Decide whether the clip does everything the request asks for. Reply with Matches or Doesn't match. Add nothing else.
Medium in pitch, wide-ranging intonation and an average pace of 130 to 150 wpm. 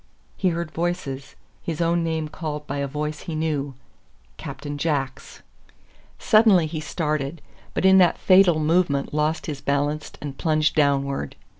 Doesn't match